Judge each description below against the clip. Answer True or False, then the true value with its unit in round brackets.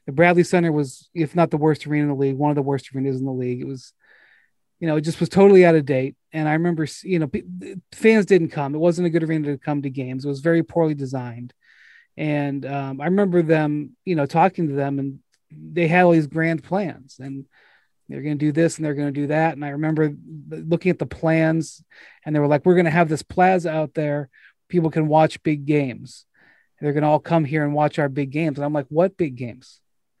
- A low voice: False (155 Hz)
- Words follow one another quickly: True (245 wpm)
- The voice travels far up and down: False (2.7 semitones)